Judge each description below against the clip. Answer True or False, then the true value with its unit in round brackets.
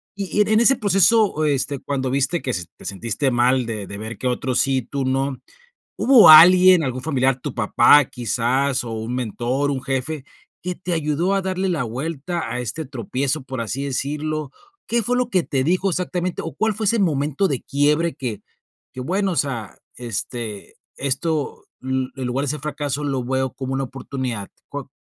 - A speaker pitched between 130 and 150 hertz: True (140 Hz)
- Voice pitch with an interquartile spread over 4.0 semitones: True (4.6 semitones)